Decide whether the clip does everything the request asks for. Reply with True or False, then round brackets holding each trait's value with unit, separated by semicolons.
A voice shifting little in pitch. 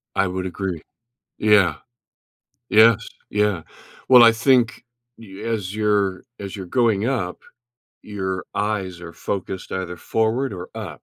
False (3.1 semitones)